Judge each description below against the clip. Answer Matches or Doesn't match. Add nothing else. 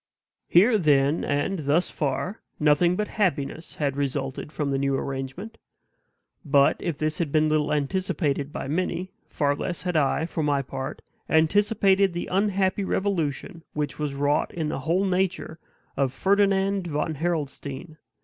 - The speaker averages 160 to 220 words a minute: Doesn't match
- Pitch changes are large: Doesn't match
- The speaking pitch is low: Doesn't match